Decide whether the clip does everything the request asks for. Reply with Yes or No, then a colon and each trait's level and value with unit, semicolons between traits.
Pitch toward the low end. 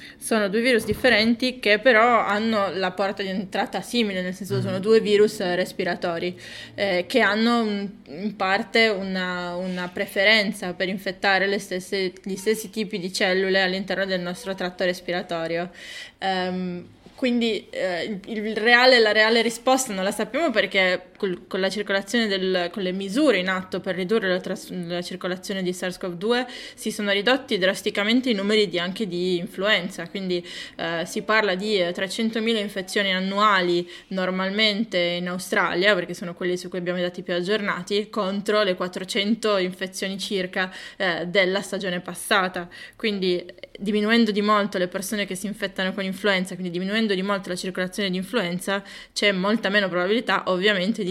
No: high, 195 Hz